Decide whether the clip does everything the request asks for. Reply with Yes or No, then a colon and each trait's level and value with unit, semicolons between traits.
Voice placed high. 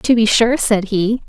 Yes: high, 220 Hz